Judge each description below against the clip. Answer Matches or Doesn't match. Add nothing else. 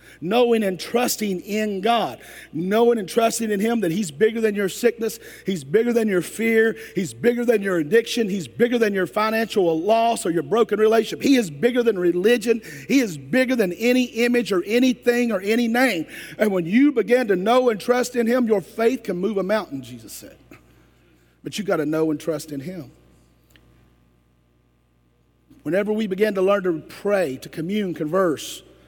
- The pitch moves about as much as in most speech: Doesn't match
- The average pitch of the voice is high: Matches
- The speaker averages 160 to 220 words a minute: Matches